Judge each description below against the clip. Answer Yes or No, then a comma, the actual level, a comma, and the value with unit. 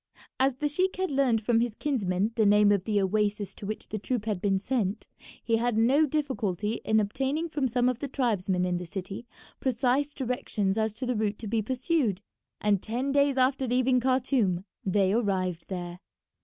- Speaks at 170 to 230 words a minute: Yes, average, 190 wpm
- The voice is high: Yes, high, 225 Hz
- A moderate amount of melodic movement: Yes, average, 4.4 semitones